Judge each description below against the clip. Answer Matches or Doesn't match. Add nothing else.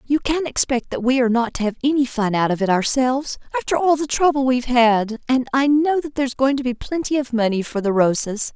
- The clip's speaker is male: Doesn't match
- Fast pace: Matches